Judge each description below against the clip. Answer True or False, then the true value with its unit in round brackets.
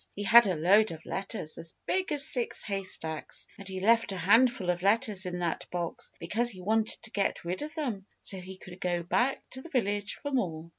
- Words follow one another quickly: True (215 wpm)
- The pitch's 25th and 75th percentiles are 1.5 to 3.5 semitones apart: False (4.7 semitones)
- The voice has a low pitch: False (195 Hz)